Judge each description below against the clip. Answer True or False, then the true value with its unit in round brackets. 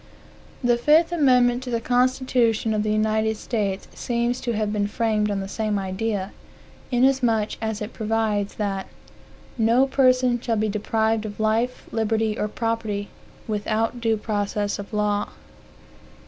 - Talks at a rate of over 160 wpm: False (145 wpm)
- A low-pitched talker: False (220 Hz)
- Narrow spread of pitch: True (2.3 semitones)